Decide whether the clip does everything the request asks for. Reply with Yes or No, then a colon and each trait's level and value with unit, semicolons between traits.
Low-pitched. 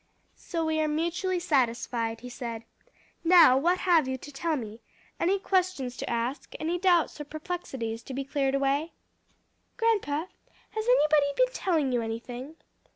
No: very high, 295 Hz